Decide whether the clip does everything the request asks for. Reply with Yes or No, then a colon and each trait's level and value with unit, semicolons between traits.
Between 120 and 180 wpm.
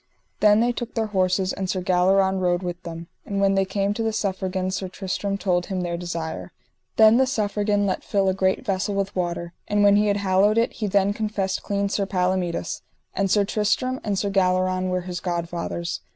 No: fast, 205 wpm